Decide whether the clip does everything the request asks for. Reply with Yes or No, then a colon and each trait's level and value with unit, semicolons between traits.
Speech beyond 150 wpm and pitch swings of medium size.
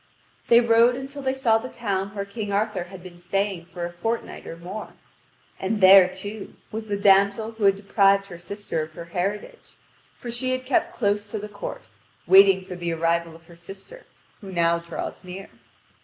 Yes: average, 190 wpm; average, 3.7 semitones